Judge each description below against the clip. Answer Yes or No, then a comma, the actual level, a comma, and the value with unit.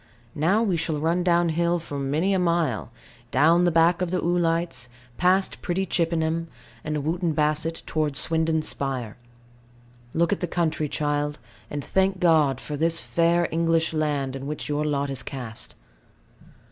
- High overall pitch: No, medium, 160 Hz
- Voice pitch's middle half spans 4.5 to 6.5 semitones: No, average, 2.7 semitones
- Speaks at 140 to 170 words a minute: Yes, average, 160 wpm